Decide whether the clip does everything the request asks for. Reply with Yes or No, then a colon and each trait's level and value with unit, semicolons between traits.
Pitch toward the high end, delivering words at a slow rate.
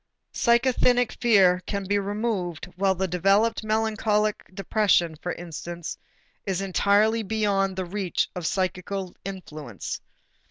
Yes: high, 195 Hz; slow, 115 wpm